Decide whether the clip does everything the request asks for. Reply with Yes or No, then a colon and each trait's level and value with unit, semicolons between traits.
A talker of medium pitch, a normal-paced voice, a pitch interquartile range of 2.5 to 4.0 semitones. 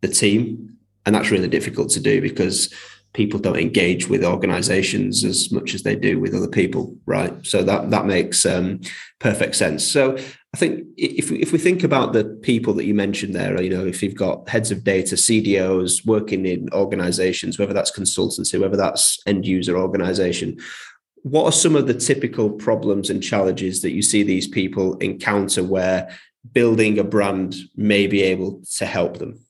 No: low, 100 Hz; average, 180 wpm; average, 3.2 semitones